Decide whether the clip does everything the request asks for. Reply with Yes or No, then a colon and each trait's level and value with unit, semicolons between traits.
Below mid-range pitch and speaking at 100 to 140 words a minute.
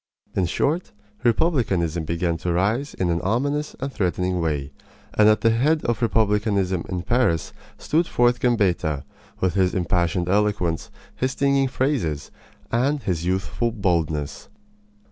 Yes: low, 100 Hz; slow, 135 wpm